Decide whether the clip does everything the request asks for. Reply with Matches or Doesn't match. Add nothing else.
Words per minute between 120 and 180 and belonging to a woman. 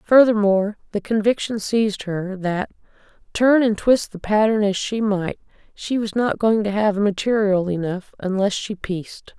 Matches